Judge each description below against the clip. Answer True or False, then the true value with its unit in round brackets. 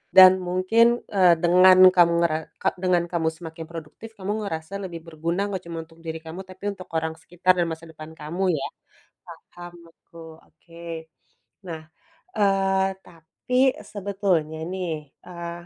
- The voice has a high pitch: False (175 Hz)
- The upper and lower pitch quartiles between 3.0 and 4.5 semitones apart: False (2.4 semitones)